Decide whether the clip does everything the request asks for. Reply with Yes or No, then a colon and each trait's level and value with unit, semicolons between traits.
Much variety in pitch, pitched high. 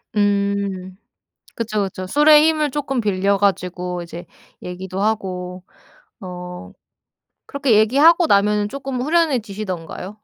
Yes: wide, 5.9 semitones; high, 205 Hz